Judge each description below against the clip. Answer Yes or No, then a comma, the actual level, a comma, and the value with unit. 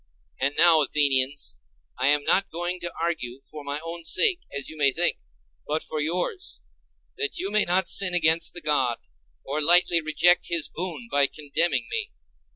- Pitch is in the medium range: Yes, medium, 160 Hz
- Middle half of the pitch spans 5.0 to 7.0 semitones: No, average, 3.6 semitones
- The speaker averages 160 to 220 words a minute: Yes, average, 170 wpm